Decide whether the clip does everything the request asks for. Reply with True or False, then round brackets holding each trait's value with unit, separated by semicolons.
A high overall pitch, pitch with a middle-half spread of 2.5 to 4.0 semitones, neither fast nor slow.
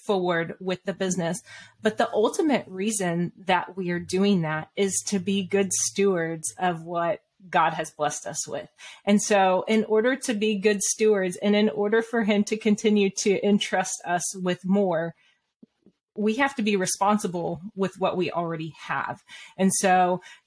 True (195 Hz; 2.9 semitones; 165 wpm)